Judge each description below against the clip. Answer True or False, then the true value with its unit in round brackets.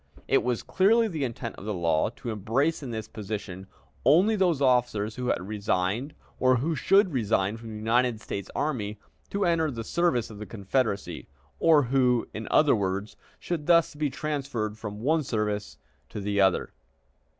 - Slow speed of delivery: False (175 wpm)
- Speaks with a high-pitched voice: False (120 Hz)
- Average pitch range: False (6.0 semitones)